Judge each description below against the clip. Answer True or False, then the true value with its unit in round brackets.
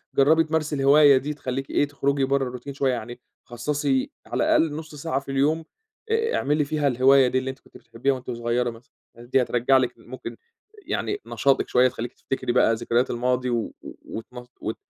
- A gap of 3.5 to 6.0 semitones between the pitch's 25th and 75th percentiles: False (2.8 semitones)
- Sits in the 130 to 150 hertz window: True (135 Hz)